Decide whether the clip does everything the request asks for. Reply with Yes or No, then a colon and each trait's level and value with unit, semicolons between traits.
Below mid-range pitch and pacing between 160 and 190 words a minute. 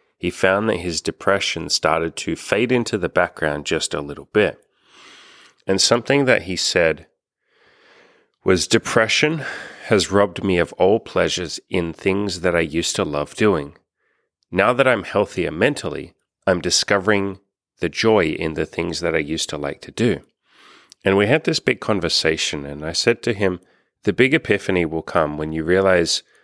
Yes: low, 100 Hz; average, 170 wpm